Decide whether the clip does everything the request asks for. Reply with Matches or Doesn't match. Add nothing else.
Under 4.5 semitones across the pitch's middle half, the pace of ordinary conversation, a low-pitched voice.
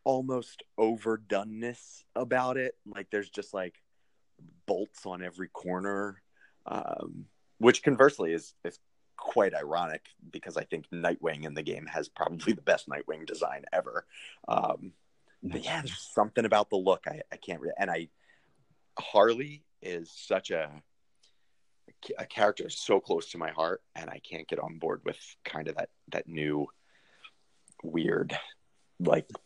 Doesn't match